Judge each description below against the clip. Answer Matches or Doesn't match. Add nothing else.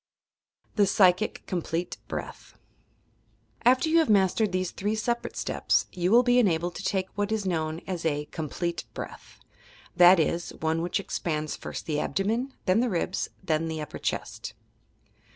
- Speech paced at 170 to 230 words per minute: Doesn't match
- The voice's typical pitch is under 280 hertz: Matches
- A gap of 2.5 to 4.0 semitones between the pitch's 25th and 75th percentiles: Doesn't match